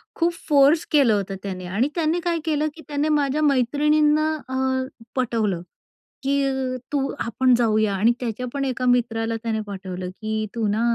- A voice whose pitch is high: Yes, very high, 255 Hz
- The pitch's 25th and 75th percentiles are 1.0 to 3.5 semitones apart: No, average, 5.2 semitones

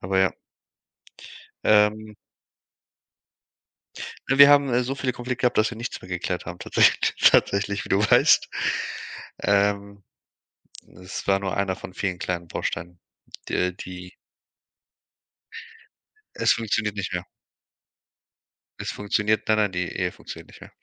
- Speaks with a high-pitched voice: No, low, 100 Hz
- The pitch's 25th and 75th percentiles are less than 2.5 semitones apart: No, average, 2.8 semitones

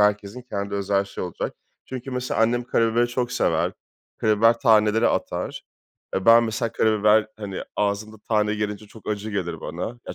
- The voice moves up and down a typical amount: No, narrow, 2.2 semitones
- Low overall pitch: Yes, low, 110 Hz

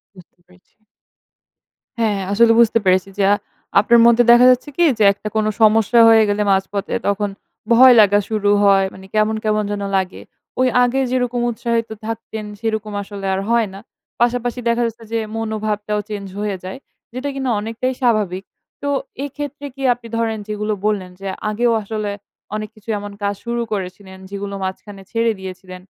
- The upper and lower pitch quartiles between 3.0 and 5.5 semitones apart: No, narrow, 2.6 semitones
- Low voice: No, high, 215 Hz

